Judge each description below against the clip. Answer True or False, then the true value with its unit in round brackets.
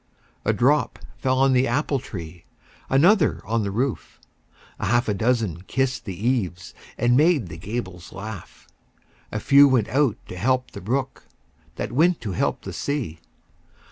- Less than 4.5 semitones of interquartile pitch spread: False (5.3 semitones)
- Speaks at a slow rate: False (160 wpm)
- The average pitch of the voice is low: True (120 Hz)